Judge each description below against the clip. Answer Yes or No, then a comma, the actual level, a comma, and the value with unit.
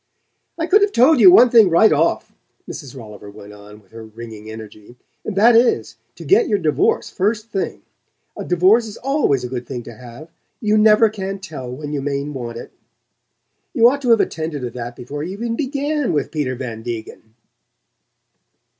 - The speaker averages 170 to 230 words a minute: Yes, average, 190 wpm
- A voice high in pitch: No, medium, 155 Hz